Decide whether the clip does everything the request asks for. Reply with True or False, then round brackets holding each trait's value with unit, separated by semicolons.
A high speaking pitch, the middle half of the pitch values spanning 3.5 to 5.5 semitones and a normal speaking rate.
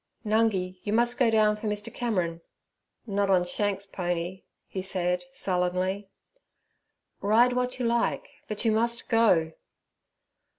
False (205 Hz; 3.8 semitones; 130 wpm)